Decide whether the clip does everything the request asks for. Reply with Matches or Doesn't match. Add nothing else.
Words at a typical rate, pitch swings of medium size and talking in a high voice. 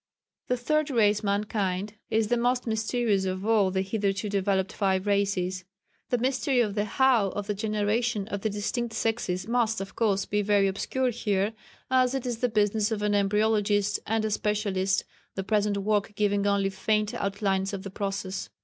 Doesn't match